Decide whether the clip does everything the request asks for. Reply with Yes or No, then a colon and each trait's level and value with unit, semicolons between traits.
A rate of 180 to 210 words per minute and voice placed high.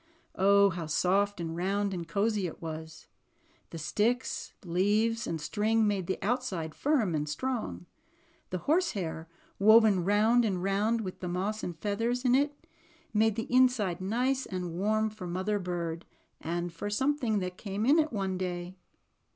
No: average, 165 wpm; high, 200 Hz